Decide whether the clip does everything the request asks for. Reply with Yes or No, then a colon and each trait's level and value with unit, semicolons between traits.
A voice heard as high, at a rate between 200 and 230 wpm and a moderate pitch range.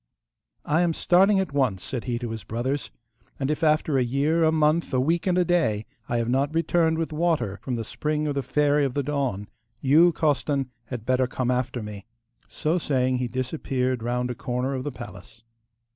No: low, 135 Hz; fast, 205 wpm; average, 4.0 semitones